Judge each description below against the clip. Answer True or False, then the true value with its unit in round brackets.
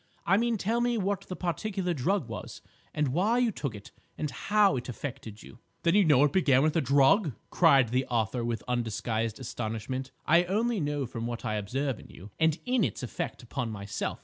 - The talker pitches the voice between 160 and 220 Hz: False (140 Hz)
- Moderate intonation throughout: False (8.0 semitones)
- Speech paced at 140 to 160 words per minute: False (200 wpm)